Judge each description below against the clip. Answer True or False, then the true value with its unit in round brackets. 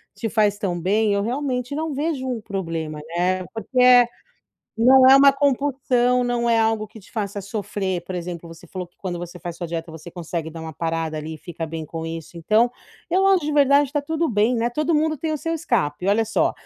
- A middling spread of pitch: False (7.2 semitones)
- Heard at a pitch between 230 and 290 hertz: False (215 Hz)